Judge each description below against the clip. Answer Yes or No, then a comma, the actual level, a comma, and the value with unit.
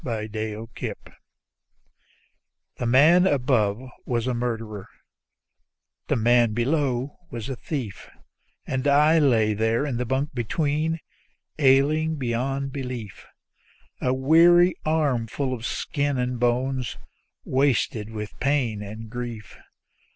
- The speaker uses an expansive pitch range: No, average, 3.7 semitones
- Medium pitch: No, low, 125 Hz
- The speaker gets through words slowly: Yes, slow, 110 wpm